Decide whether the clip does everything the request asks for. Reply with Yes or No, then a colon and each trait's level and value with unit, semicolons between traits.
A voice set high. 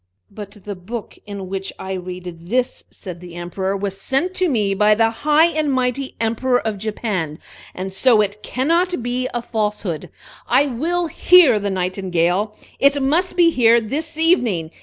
Yes: high, 220 Hz